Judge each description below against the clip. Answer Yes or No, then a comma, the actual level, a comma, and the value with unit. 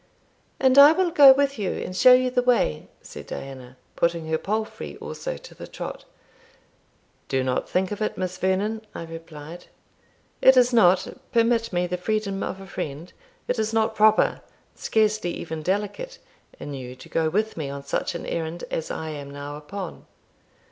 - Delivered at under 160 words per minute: No, average, 175 wpm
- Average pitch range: No, wide, 6.1 semitones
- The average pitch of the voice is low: No, high, 190 Hz